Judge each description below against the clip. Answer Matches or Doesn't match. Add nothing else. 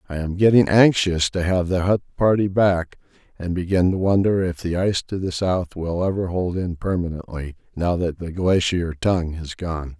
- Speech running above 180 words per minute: Matches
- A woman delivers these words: Doesn't match